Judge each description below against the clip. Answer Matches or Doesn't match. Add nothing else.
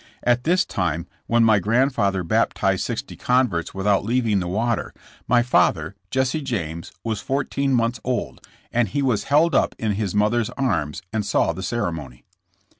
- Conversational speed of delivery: Matches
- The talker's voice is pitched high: Doesn't match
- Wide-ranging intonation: Doesn't match